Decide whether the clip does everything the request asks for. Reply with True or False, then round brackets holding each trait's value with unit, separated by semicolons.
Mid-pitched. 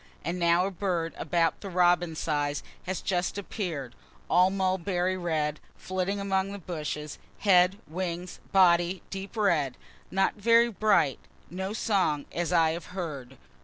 True (180 Hz)